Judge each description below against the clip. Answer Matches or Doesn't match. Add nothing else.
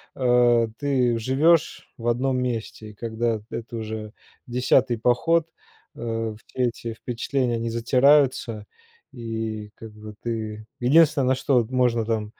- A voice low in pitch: Matches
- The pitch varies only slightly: Matches